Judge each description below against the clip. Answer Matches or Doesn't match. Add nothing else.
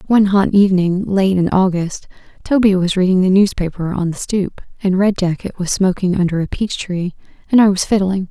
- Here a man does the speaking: Doesn't match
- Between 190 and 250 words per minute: Matches